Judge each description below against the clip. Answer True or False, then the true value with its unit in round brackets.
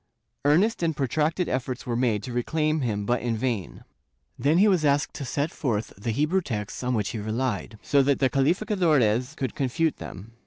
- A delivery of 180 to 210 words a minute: True (190 wpm)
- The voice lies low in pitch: True (130 Hz)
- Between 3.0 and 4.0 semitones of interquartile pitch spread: False (4.9 semitones)